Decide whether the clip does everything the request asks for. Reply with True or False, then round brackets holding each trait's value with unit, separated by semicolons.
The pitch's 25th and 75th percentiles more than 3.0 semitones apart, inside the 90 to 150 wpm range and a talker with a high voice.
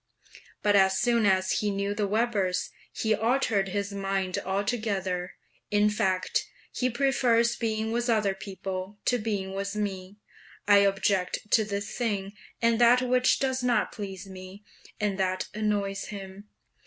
False (2.7 semitones; 145 wpm; 205 Hz)